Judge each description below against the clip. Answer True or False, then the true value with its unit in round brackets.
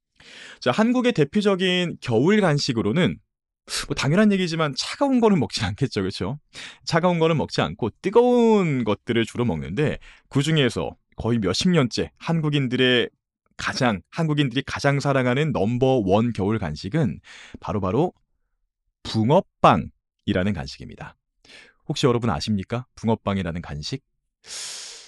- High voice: False (135 Hz)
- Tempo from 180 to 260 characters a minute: False (300 characters per minute)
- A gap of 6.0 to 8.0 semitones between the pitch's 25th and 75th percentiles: True (6.6 semitones)